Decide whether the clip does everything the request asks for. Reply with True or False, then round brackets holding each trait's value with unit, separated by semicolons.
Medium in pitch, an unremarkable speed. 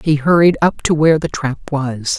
False (150 Hz; 220 wpm)